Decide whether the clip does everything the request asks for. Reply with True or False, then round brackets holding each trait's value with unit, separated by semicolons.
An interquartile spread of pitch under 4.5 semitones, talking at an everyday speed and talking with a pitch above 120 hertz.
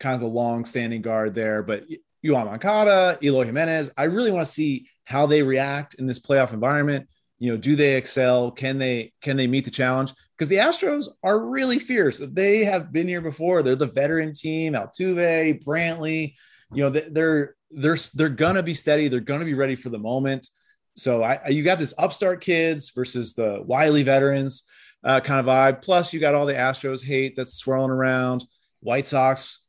True (3.7 semitones; 190 wpm; 140 Hz)